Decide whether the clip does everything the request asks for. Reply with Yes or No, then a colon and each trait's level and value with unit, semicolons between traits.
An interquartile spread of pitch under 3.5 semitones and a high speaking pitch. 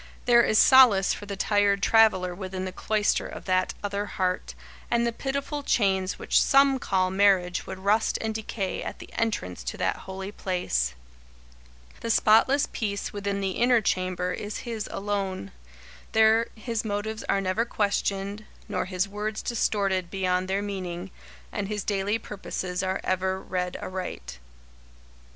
Yes: average, 2.7 semitones; high, 200 Hz